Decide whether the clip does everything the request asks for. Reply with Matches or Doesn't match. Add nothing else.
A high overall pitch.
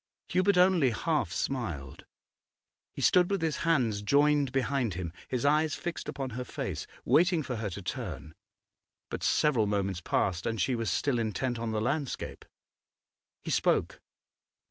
Doesn't match